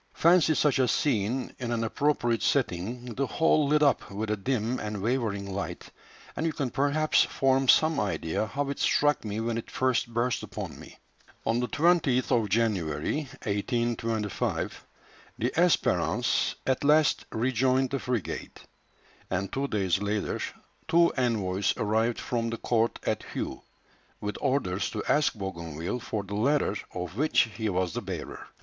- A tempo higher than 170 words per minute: No, average, 155 wpm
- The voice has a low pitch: Yes, low, 115 Hz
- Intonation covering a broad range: No, average, 4.7 semitones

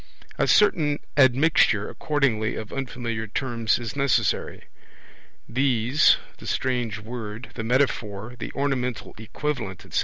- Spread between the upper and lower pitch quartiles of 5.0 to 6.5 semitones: No, average, 3.8 semitones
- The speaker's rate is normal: No, slow, 115 wpm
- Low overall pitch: Yes, low, 125 Hz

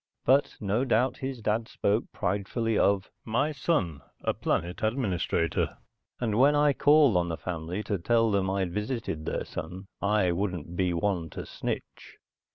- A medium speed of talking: Yes, average, 160 wpm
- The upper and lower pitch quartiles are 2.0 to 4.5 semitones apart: No, average, 4.9 semitones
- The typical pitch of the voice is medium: No, low, 105 Hz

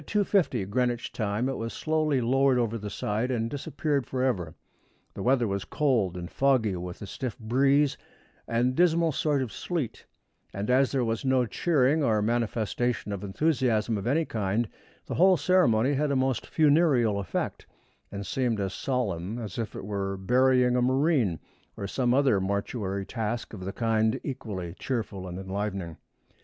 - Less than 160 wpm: No, average, 165 wpm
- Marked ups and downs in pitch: No, average, 4.8 semitones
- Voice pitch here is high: No, low, 120 Hz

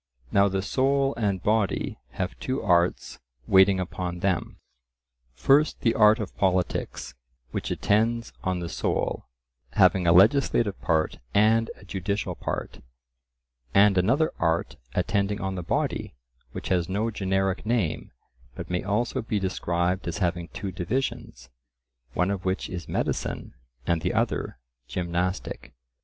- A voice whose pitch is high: No, very low, 95 Hz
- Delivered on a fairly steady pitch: No, average, 3.2 semitones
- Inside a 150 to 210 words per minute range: No, slow, 135 wpm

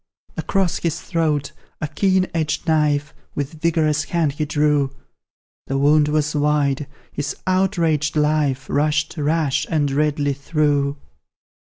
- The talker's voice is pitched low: No, medium, 150 Hz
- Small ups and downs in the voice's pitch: Yes, narrow, 1.7 semitones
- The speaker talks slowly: Yes, slow, 120 wpm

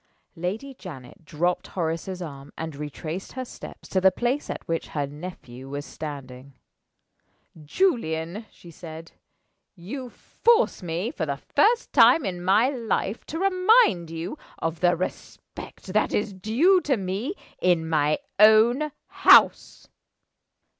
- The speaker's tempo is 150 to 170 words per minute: No, slow, 135 wpm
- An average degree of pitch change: No, wide, 7.0 semitones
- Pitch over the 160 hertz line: Yes, medium, 185 Hz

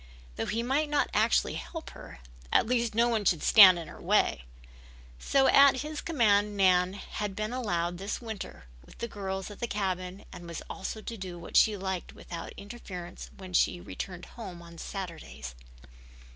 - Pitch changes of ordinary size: Yes, average, 4.4 semitones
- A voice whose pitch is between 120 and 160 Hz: No, high, 195 Hz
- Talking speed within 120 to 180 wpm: Yes, average, 175 wpm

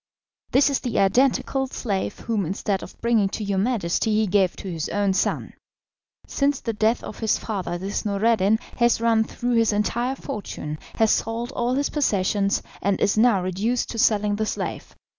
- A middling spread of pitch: Yes, average, 3.2 semitones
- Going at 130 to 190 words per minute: Yes, average, 180 wpm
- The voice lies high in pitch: Yes, high, 215 Hz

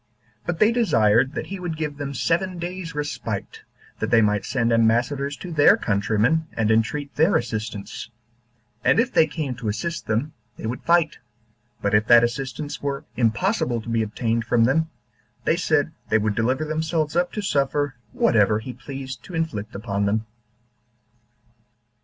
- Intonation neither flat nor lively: No, wide, 6.0 semitones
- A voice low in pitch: Yes, low, 130 Hz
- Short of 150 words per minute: No, average, 165 wpm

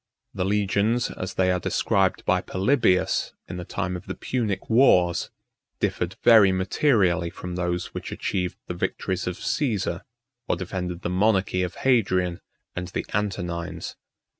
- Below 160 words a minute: Yes, average, 150 wpm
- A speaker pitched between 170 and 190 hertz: No, very low, 95 Hz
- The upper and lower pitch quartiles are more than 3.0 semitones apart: No, narrow, 2.6 semitones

